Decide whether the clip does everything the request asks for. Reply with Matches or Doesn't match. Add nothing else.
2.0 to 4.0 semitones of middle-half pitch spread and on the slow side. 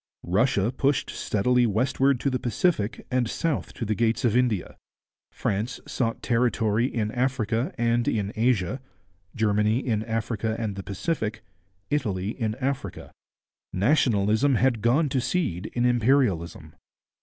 Matches